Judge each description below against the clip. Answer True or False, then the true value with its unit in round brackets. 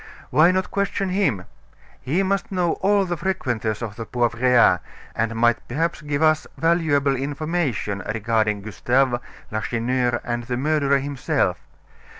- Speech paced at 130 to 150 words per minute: True (135 wpm)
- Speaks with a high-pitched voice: False (135 Hz)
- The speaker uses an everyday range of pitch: False (6.0 semitones)